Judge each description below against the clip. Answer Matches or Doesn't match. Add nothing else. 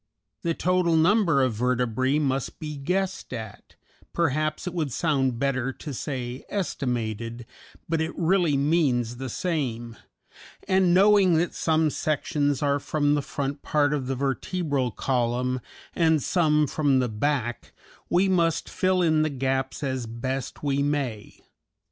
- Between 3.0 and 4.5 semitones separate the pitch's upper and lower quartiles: Matches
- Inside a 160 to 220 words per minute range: Doesn't match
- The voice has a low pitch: Doesn't match